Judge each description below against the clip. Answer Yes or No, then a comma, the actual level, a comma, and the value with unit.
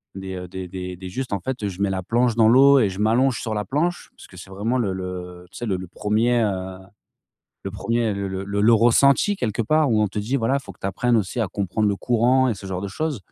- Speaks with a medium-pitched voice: No, low, 105 Hz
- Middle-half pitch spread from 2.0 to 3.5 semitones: No, average, 4.2 semitones